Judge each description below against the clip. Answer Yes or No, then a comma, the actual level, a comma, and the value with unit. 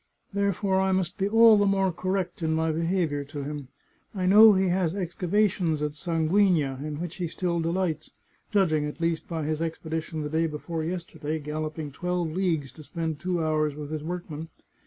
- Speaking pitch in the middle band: Yes, medium, 165 Hz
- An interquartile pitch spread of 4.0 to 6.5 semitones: No, average, 3.1 semitones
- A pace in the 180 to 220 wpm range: Yes, average, 190 wpm